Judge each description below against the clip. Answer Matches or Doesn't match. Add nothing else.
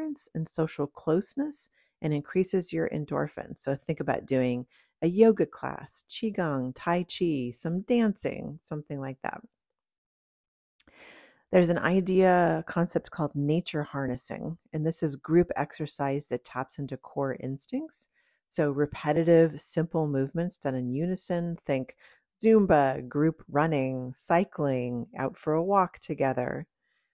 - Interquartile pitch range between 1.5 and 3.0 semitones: Doesn't match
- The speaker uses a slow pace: Matches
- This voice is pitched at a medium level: Matches